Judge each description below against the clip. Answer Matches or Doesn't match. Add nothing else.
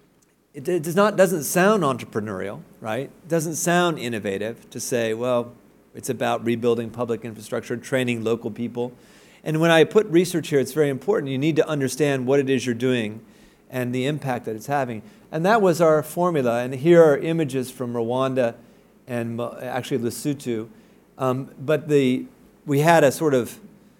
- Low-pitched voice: Matches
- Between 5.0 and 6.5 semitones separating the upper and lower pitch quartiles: Matches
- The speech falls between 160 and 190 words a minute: Matches